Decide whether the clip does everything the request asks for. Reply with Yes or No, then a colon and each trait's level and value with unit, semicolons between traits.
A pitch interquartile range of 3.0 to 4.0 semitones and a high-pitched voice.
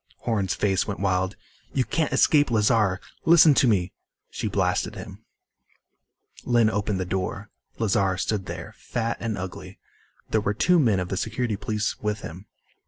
No: average, 3.3 semitones; low, 105 Hz